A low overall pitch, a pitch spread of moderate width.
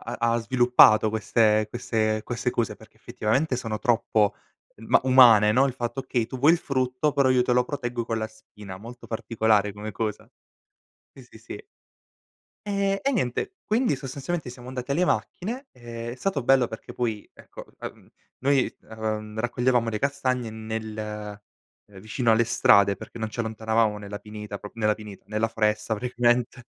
Yes: low, 115 Hz; average, 3.0 semitones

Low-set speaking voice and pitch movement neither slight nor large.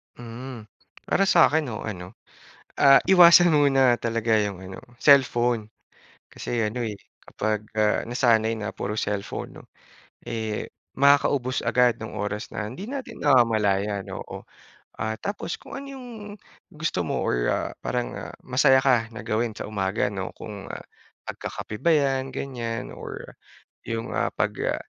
Yes: low, 115 Hz; average, 4.2 semitones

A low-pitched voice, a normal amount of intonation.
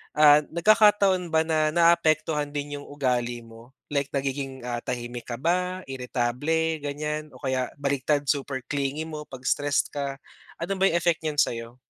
No: medium, 145 Hz; average, 3.3 semitones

